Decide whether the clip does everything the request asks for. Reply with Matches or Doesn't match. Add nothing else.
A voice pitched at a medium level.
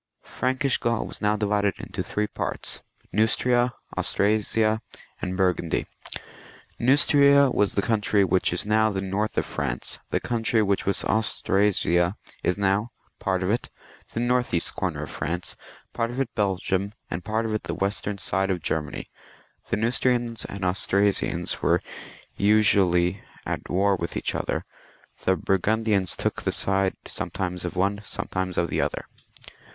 Doesn't match